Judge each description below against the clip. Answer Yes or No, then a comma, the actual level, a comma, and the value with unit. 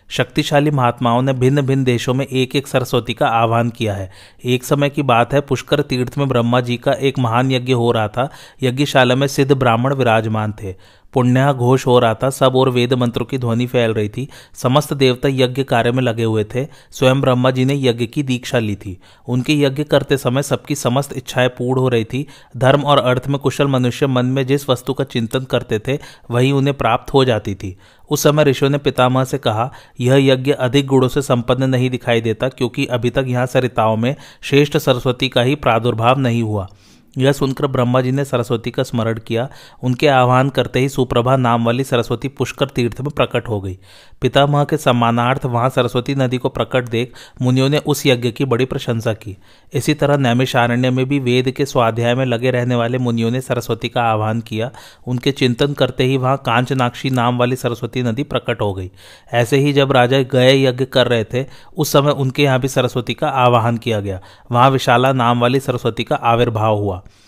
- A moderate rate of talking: No, fast, 200 wpm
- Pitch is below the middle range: Yes, low, 125 Hz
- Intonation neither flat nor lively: No, narrow, 2.3 semitones